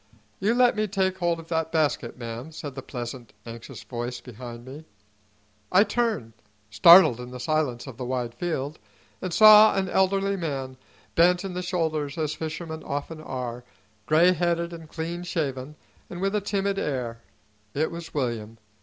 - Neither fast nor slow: Yes, average, 165 wpm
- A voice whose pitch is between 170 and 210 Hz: No, medium, 155 Hz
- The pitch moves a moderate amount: No, wide, 6.0 semitones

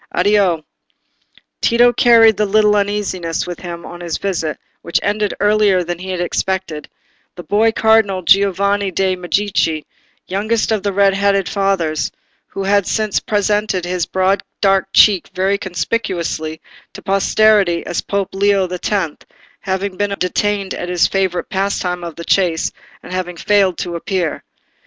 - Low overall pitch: No, high, 195 Hz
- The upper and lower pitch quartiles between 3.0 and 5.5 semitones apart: No, narrow, 2.4 semitones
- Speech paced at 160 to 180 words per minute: No, average, 145 wpm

